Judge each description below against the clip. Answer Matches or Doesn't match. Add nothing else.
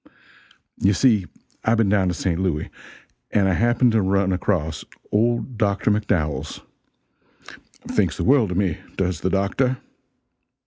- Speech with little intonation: Doesn't match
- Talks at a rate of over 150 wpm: Doesn't match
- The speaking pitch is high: Doesn't match